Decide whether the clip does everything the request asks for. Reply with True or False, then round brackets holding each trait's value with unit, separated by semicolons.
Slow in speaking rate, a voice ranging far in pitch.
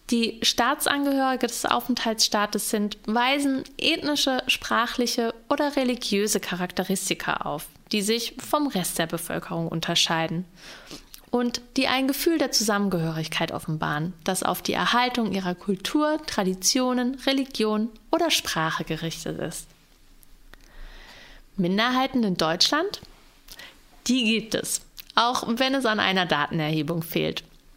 True (110 wpm; 6.3 semitones)